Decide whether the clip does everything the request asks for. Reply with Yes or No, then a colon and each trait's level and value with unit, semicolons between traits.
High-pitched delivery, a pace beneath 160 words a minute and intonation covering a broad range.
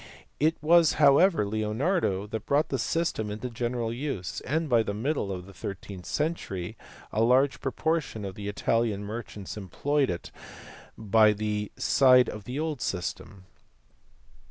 No: low, 115 Hz; average, 150 wpm; wide, 5.7 semitones